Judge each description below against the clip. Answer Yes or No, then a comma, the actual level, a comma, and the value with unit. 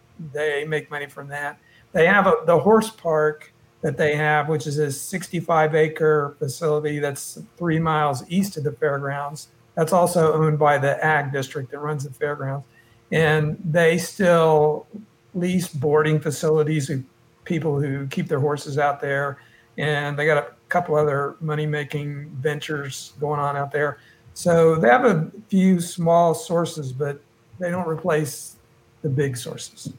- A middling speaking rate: Yes, average, 155 wpm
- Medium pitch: Yes, medium, 150 Hz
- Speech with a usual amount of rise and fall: No, narrow, 2.1 semitones